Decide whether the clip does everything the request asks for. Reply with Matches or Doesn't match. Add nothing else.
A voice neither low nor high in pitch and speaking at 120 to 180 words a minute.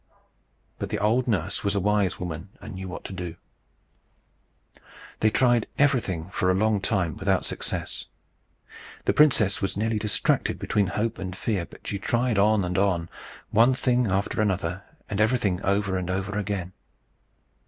Doesn't match